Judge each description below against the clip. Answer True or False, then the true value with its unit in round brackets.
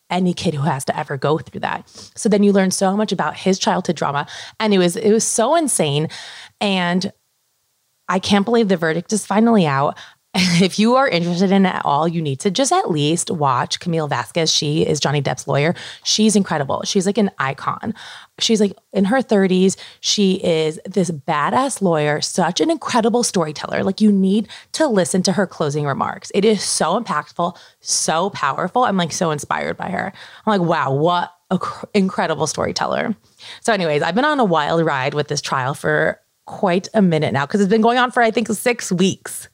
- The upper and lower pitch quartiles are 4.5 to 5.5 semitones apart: True (4.9 semitones)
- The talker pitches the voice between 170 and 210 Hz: True (185 Hz)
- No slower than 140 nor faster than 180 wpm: False (200 wpm)